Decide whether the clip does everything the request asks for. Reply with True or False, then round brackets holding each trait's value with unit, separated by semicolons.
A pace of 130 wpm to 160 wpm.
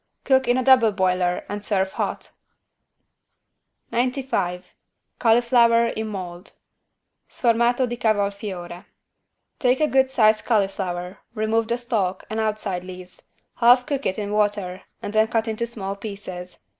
True (135 wpm)